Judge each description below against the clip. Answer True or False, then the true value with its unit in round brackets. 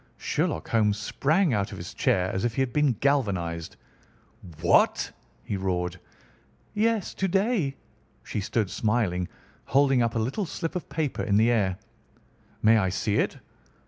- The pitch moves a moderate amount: False (6.8 semitones)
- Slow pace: False (155 wpm)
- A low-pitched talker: True (115 Hz)